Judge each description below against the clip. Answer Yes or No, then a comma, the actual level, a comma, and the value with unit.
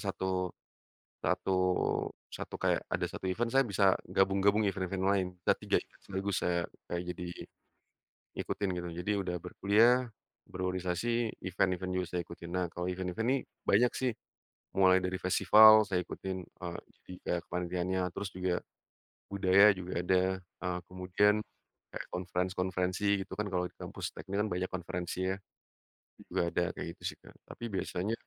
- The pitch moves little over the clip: Yes, narrow, 1.8 semitones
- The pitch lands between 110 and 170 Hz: No, very low, 95 Hz